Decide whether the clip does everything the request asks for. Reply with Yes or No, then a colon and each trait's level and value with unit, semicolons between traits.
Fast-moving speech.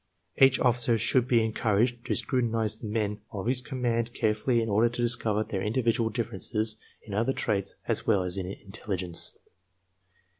No: average, 165 wpm